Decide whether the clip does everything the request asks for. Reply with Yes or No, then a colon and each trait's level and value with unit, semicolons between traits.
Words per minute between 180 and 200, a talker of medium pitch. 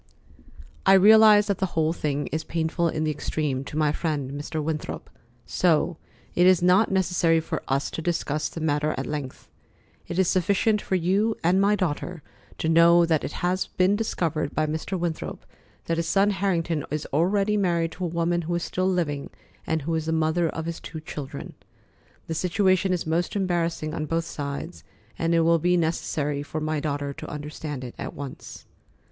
Yes: average, 190 wpm; medium, 165 Hz